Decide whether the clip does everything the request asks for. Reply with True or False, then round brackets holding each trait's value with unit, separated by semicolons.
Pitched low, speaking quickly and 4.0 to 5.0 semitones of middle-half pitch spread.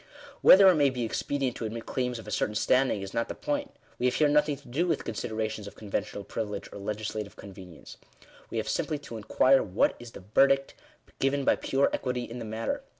True (120 Hz; 215 wpm; 4.3 semitones)